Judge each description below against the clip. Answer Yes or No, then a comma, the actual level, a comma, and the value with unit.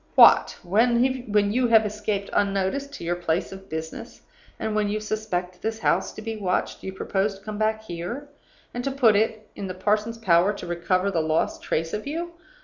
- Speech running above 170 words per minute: Yes, average, 195 wpm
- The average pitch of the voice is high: Yes, high, 210 Hz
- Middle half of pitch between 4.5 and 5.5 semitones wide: No, average, 3.3 semitones